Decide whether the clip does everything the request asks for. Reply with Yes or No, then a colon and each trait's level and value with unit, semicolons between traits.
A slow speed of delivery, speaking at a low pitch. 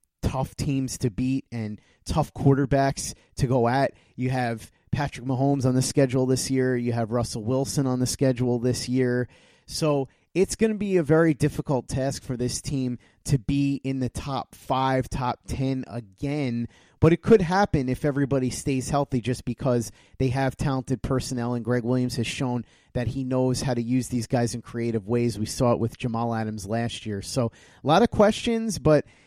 No: average, 190 wpm; low, 130 Hz